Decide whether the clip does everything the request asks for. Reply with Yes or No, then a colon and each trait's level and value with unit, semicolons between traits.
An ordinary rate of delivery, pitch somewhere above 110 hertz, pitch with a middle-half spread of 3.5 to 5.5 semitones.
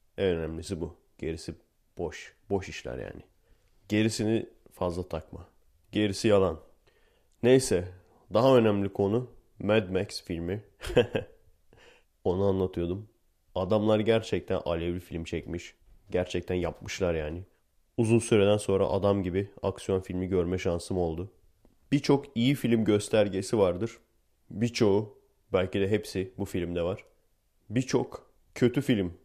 No: average, 115 wpm; very low, 95 Hz; average, 3.8 semitones